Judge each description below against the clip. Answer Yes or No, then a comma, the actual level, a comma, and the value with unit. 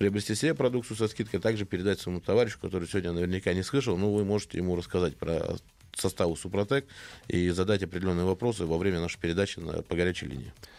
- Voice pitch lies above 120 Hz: No, very low, 95 Hz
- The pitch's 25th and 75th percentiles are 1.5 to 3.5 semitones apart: Yes, average, 2.9 semitones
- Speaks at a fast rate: Yes, fast, 190 wpm